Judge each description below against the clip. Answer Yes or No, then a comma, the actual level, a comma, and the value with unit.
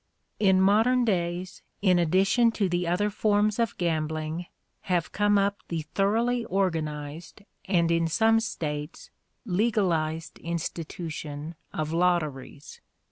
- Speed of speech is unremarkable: No, slow, 115 wpm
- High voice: No, medium, 175 Hz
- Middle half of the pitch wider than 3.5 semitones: Yes, average, 4.2 semitones